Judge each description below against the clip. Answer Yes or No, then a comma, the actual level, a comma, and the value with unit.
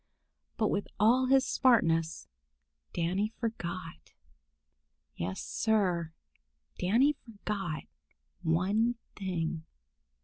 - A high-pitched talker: Yes, high, 195 Hz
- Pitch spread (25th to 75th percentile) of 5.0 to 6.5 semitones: Yes, wide, 5.4 semitones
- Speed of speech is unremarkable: No, slow, 75 wpm